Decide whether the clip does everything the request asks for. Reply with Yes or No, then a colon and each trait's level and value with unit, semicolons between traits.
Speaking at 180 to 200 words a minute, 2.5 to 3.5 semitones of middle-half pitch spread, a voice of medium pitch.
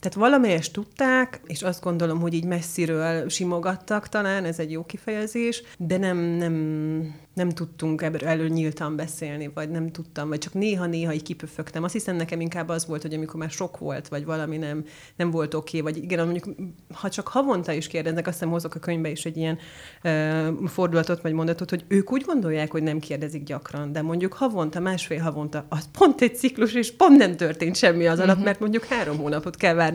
Yes: fast, 195 wpm; average, 2.8 semitones; medium, 165 Hz